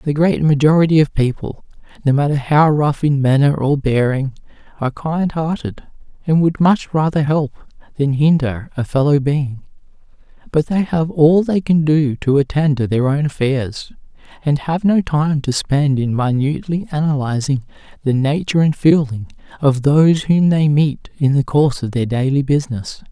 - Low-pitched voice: No, medium, 145 Hz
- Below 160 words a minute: No, average, 165 wpm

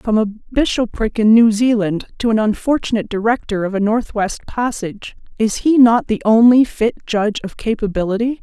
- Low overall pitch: No, high, 220 Hz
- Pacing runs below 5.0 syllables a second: No, 5.2 syllables/s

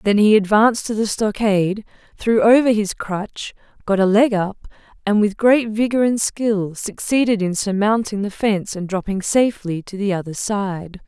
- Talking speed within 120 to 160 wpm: No, average, 175 wpm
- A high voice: Yes, high, 210 Hz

